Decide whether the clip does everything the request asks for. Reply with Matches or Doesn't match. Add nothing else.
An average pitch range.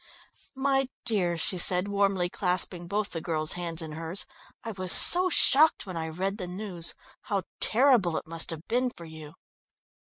Matches